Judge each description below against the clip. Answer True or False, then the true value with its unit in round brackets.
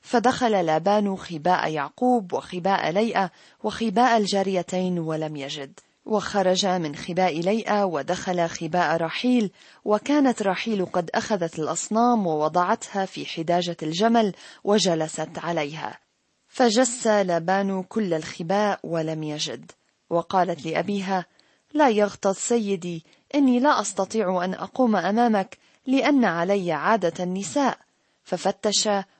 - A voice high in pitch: True (195 Hz)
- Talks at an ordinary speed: True (105 wpm)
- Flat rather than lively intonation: False (4.3 semitones)